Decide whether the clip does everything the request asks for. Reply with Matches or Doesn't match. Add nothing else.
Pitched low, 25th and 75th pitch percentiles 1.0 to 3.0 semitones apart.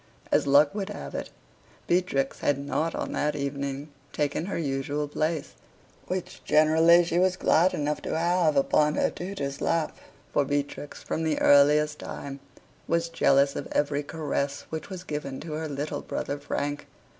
Doesn't match